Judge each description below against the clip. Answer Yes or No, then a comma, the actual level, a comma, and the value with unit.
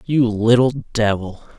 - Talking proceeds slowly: Yes, slow, 115 wpm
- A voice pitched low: Yes, low, 115 Hz